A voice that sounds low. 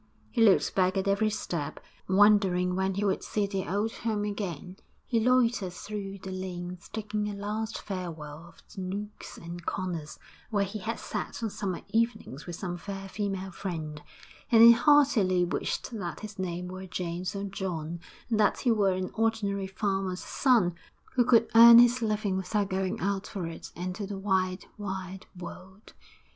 No: high, 195 Hz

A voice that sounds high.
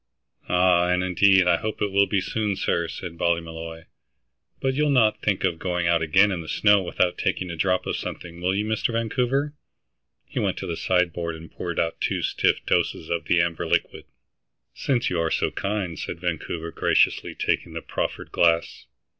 No: very low, 90 Hz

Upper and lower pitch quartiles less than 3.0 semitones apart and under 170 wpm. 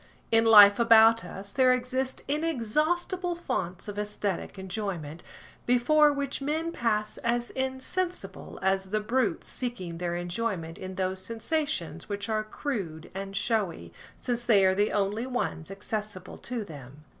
No: average, 5.0 semitones; average, 140 wpm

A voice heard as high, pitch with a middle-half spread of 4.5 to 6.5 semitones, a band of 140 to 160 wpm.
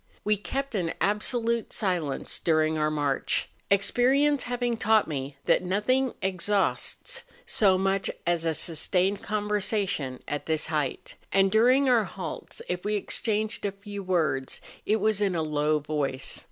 Yes: high, 195 Hz; average, 5.3 semitones; average, 145 wpm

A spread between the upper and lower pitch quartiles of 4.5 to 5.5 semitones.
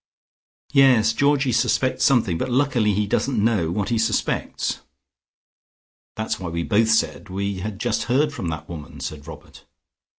Yes: average, 5.2 semitones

